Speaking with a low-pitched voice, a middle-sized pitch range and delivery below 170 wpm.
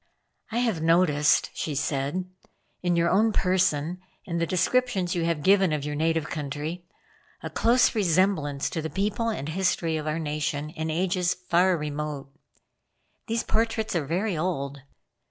No: medium, 170 Hz; average, 3.8 semitones; average, 155 wpm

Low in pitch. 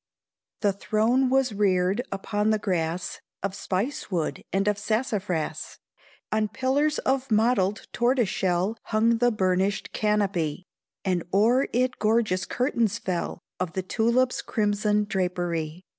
No: high, 210 Hz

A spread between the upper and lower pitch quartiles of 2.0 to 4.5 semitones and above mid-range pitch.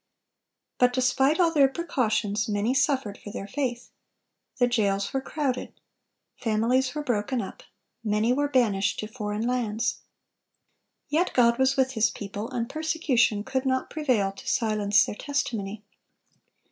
Yes: average, 4.0 semitones; high, 245 Hz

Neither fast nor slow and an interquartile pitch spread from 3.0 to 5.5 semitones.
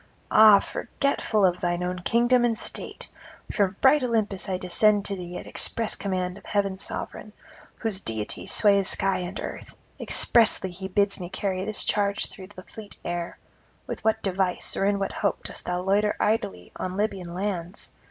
No: average, 170 wpm; narrow, 2.6 semitones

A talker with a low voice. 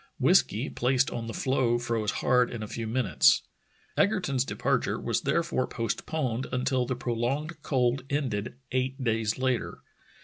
Yes: low, 125 Hz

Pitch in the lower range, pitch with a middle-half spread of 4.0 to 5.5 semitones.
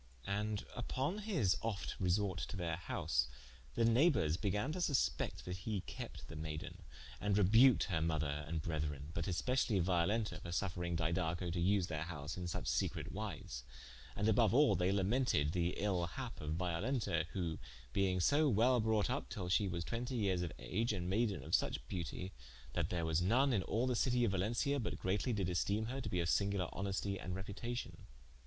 Yes: very low, 95 Hz; average, 4.8 semitones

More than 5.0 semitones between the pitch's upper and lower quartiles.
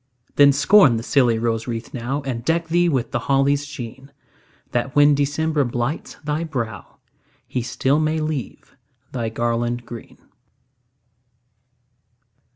No: average, 3.8 semitones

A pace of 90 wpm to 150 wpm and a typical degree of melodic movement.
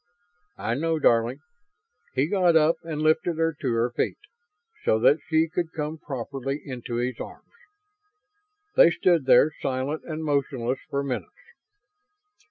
Yes: average, 140 wpm; average, 3.9 semitones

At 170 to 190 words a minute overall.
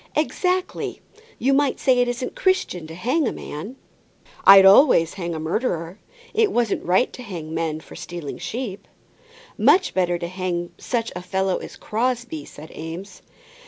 No: average, 155 wpm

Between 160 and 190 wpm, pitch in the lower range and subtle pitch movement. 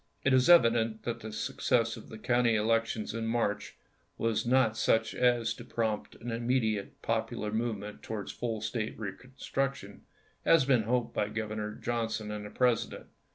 Yes: average, 165 wpm; low, 115 Hz; narrow, 2.0 semitones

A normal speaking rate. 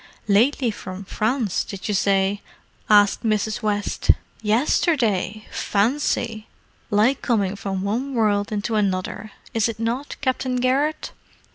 No: slow, 120 wpm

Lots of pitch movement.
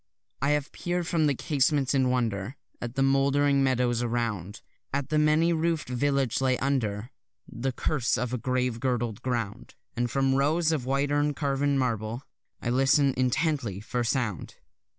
No: average, 3.0 semitones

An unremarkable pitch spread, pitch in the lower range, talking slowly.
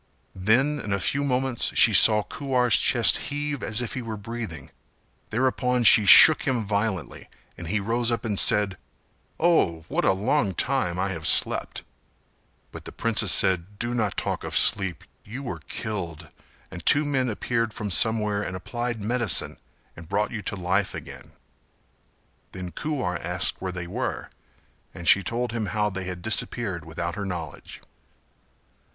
No: average, 4.7 semitones; low, 105 Hz; average, 160 wpm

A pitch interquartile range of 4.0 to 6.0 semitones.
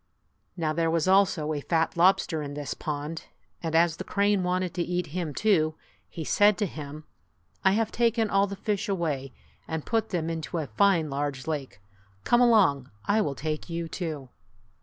Yes: average, 4.4 semitones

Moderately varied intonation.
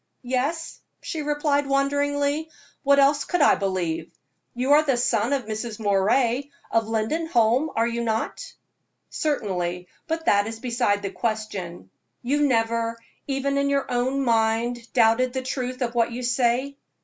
Yes: average, 4.0 semitones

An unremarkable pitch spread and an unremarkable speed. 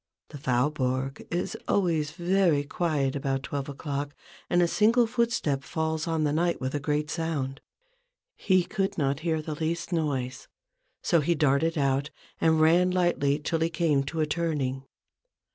Yes: average, 3.3 semitones; average, 160 wpm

